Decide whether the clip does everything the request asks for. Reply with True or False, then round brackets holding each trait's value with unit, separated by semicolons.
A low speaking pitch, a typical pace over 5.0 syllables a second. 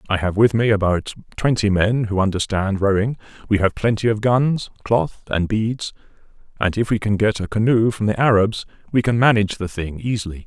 True (105 Hz; 5.3 syllables/s)